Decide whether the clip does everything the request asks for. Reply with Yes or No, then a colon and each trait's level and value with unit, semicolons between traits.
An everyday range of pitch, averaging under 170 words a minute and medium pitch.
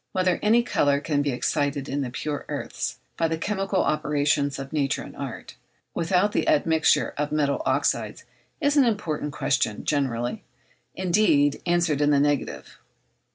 Yes: average, 4.3 semitones; average, 155 wpm; medium, 150 Hz